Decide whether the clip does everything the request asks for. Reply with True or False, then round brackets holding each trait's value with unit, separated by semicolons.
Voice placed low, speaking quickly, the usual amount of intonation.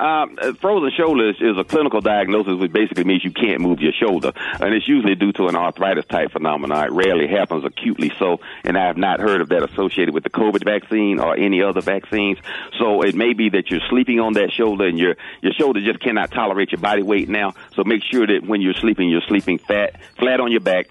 True (105 Hz; 230 wpm; 3.4 semitones)